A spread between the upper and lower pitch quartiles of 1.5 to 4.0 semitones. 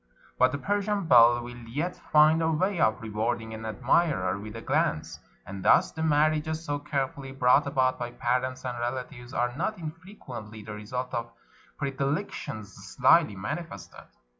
No: average, 5.0 semitones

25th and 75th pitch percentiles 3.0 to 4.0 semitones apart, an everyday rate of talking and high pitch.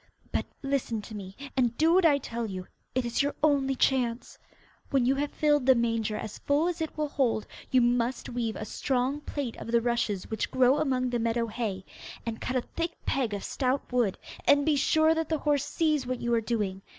No: average, 3.7 semitones; fast, 215 wpm; very high, 250 Hz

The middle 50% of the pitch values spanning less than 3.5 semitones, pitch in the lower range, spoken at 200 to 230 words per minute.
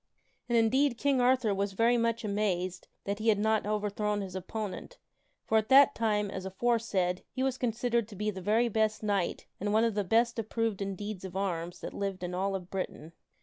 No: average, 3.0 semitones; high, 210 Hz; fast, 205 wpm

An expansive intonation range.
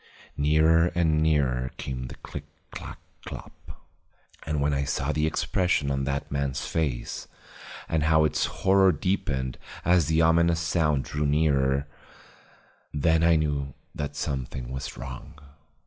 No: average, 2.9 semitones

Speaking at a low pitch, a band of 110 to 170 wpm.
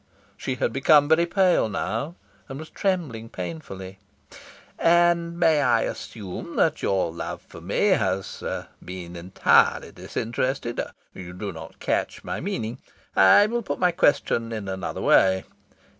Yes: low, 115 Hz; average, 140 wpm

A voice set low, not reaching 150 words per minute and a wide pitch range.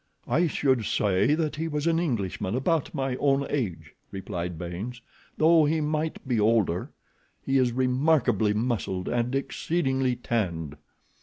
Yes: low, 125 Hz; slow, 135 wpm; wide, 6.2 semitones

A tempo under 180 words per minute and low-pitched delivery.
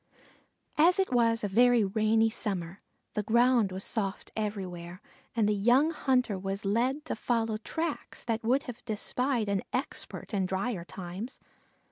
No: average, 150 wpm; high, 220 Hz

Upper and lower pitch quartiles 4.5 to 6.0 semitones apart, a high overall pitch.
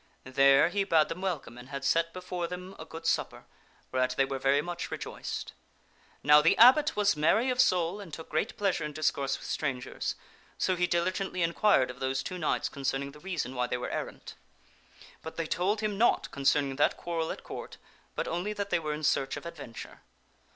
No: average, 5.0 semitones; medium, 165 Hz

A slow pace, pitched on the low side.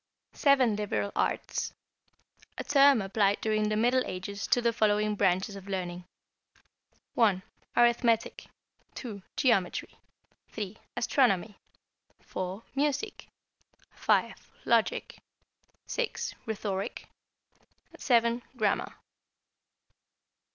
No: slow, 90 wpm; high, 215 Hz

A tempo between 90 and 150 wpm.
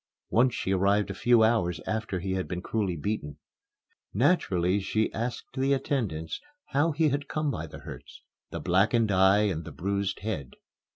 No: average, 165 wpm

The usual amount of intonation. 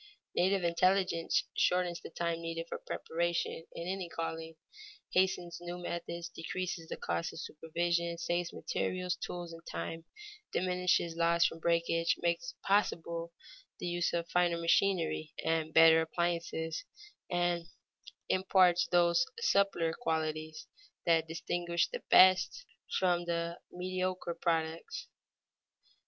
No: narrow, 1.3 semitones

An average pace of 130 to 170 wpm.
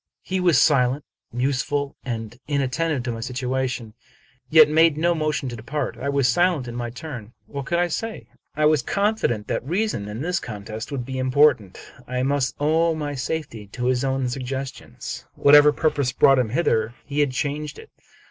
No: average, 180 wpm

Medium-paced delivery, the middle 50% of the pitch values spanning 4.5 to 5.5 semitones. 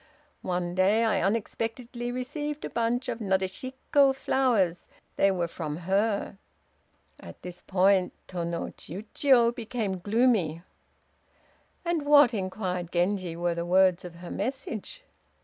No: slow, 125 wpm; average, 5.2 semitones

